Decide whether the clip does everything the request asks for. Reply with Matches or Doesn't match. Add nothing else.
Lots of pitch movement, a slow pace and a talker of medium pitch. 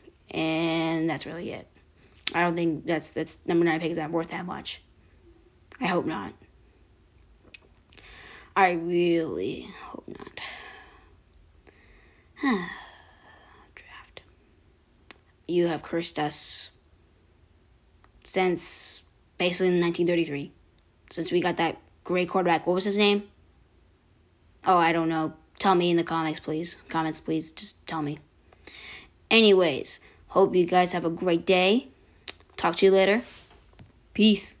Doesn't match